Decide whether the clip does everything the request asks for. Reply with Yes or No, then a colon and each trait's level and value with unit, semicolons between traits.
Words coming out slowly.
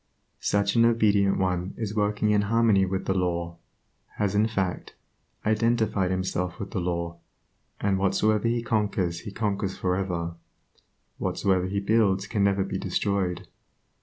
No: average, 145 wpm